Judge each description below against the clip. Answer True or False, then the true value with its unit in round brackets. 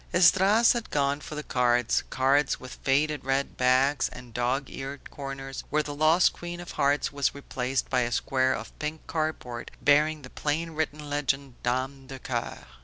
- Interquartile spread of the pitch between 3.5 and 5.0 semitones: False (2.7 semitones)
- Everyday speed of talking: True (175 wpm)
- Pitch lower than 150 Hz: True (140 Hz)